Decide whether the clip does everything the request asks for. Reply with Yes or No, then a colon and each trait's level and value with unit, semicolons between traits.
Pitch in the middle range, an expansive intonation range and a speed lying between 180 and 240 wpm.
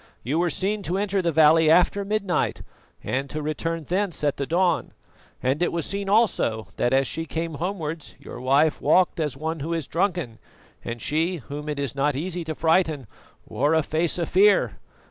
No: medium, 160 Hz; average, 3.7 semitones; average, 190 wpm